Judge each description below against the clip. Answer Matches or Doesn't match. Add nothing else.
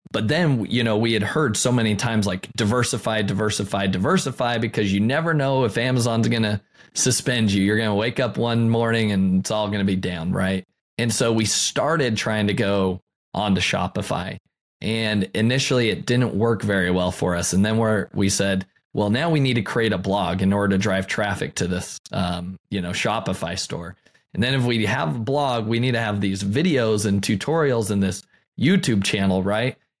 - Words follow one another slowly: Doesn't match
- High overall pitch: Doesn't match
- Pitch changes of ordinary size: Matches